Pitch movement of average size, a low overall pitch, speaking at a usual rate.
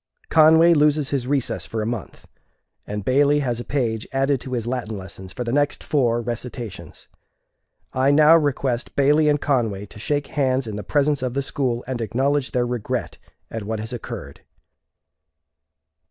Yes: average, 3.8 semitones; low, 130 Hz; average, 170 wpm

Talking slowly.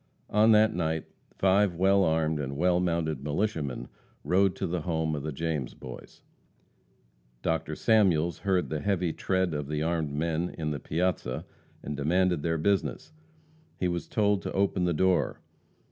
No: average, 160 wpm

